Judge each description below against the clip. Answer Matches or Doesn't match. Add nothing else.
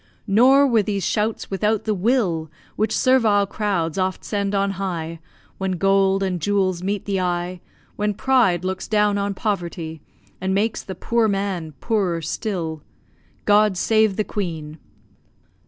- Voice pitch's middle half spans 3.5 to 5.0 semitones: Doesn't match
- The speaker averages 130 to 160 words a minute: Matches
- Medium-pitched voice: Doesn't match